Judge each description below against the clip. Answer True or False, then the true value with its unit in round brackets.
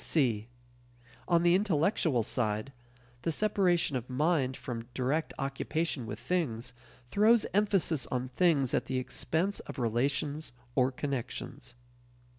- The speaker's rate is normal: False (120 wpm)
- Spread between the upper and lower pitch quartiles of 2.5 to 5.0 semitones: False (5.5 semitones)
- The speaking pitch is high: False (140 Hz)